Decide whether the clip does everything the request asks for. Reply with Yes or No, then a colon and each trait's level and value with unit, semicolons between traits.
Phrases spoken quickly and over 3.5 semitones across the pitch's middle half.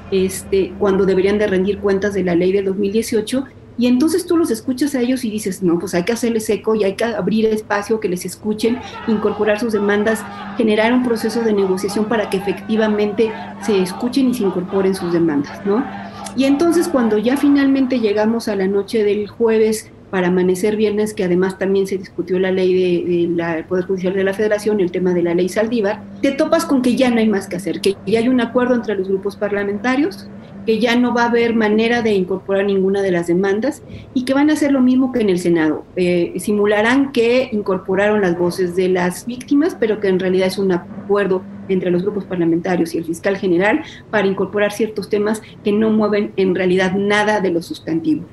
No: fast, 210 wpm; average, 3.2 semitones